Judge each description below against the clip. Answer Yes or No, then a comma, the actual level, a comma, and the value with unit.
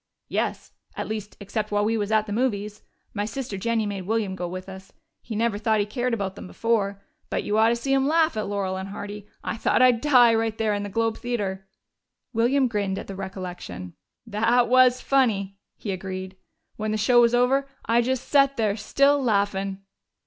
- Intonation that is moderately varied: Yes, average, 3.2 semitones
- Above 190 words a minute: Yes, average, 200 wpm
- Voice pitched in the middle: No, high, 215 Hz